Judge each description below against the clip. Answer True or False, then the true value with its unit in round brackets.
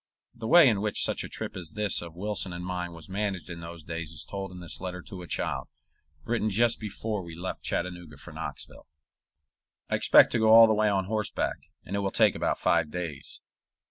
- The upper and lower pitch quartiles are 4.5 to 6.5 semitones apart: False (3.7 semitones)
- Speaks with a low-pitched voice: True (95 Hz)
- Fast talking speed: True (215 wpm)